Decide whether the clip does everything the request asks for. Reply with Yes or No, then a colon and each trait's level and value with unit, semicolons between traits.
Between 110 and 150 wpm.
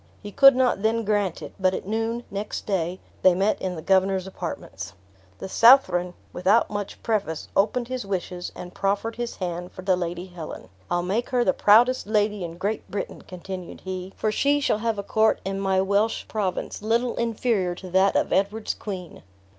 No: average, 185 wpm